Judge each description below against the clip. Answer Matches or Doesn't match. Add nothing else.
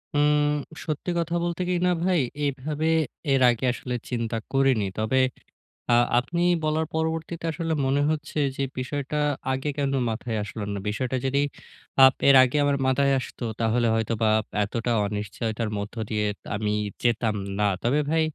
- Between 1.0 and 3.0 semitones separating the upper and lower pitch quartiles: Doesn't match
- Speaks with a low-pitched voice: Matches